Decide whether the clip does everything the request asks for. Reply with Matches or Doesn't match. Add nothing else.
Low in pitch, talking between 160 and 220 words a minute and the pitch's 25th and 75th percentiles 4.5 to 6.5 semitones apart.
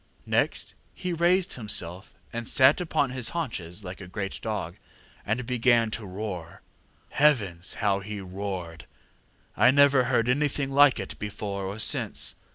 Doesn't match